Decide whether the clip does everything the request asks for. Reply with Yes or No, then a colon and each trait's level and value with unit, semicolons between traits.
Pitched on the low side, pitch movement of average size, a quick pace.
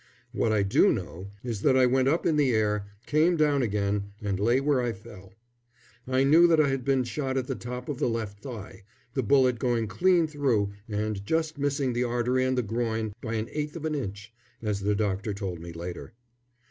Yes: low, 120 Hz; average, 4.8 semitones; fast, 210 wpm